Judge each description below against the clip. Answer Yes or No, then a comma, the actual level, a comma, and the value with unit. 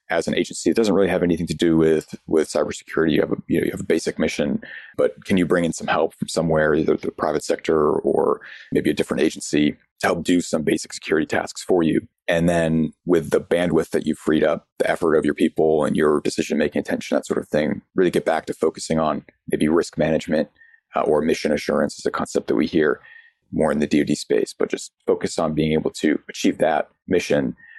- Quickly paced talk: Yes, fast, 230 wpm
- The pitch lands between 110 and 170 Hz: No, very low, 95 Hz